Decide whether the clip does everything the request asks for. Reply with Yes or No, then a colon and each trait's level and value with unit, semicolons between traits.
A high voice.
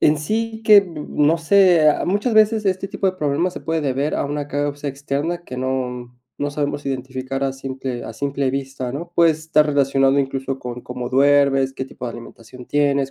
No: medium, 140 Hz